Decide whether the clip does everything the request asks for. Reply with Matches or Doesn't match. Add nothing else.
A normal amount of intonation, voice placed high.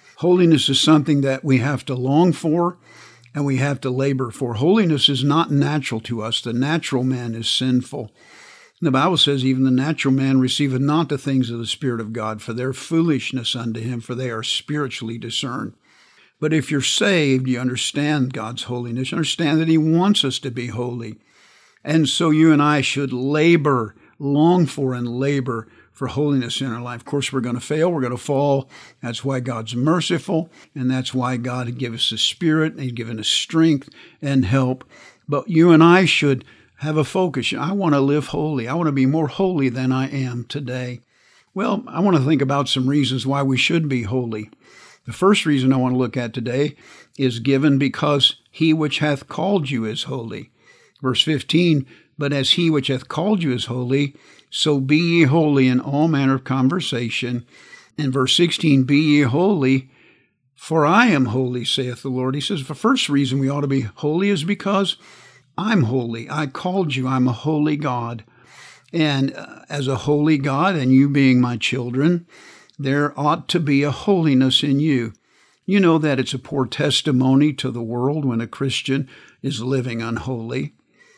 Doesn't match